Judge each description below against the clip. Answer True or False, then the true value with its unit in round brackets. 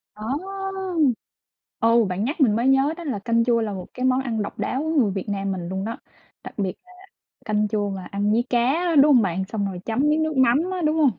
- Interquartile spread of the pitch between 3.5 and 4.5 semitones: False (4.9 semitones)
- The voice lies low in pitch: False (230 Hz)